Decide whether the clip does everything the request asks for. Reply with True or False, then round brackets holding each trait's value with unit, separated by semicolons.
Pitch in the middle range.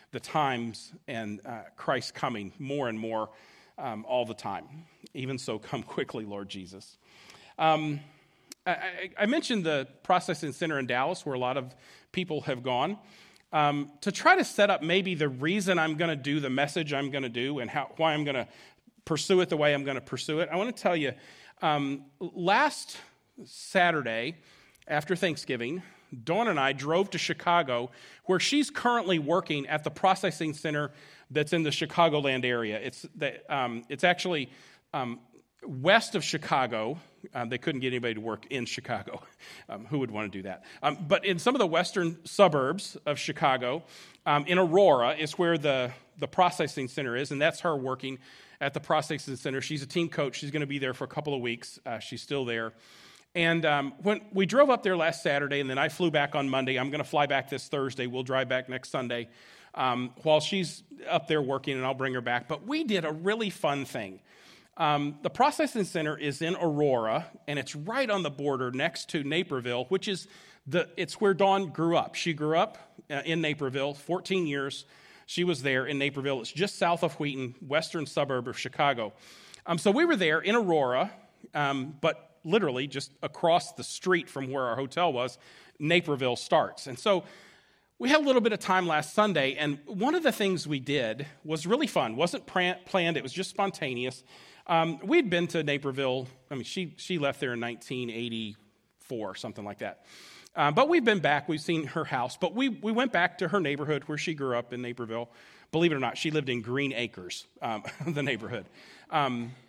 True (150 Hz)